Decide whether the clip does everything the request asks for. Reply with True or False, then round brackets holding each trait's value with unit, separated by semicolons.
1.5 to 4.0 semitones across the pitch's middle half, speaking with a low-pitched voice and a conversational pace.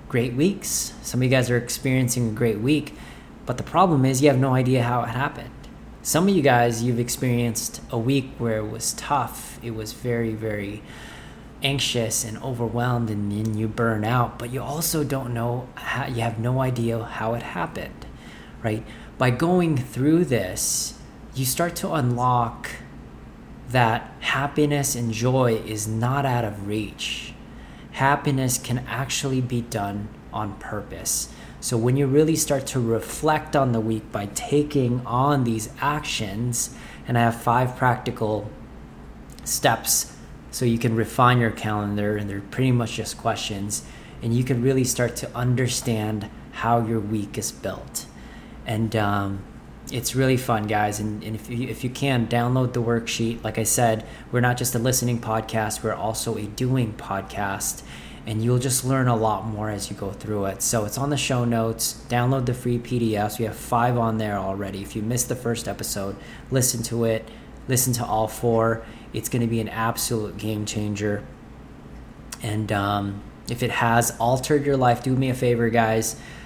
True (2.6 semitones; 120 Hz; 170 wpm)